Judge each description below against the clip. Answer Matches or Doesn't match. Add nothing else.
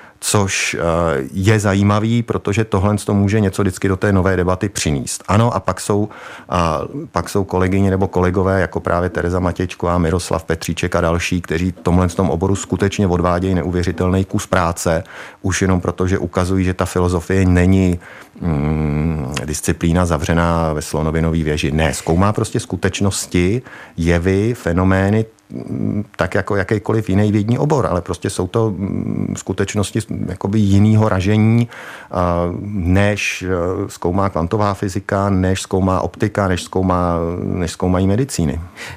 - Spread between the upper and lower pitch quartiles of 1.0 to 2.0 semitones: Doesn't match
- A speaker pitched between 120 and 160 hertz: Doesn't match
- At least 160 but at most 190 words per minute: Doesn't match